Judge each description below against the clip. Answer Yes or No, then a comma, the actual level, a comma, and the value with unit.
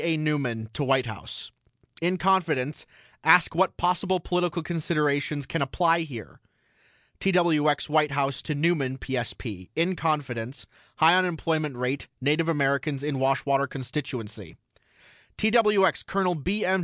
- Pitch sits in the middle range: Yes, medium, 150 Hz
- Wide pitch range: No, average, 4.3 semitones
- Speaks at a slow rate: Yes, slow, 125 wpm